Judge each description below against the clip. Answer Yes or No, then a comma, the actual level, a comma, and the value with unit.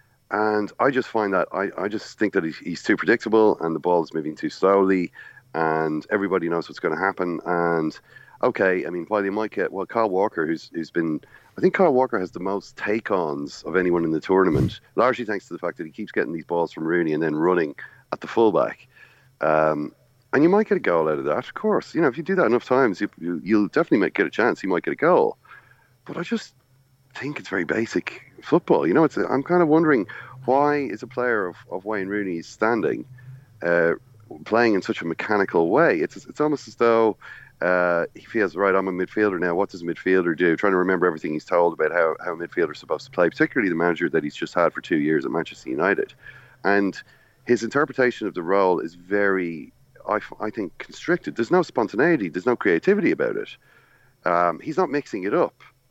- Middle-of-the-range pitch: No, low, 105 Hz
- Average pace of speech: No, fast, 230 wpm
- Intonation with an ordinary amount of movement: No, wide, 7.1 semitones